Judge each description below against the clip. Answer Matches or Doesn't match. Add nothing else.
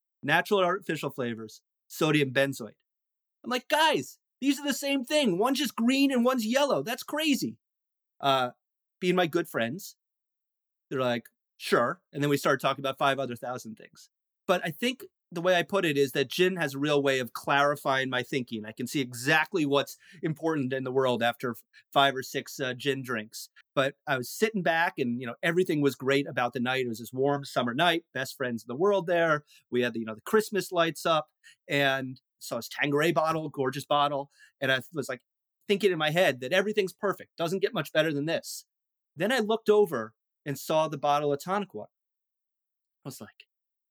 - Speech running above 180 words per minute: Matches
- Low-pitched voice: Doesn't match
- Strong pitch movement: Matches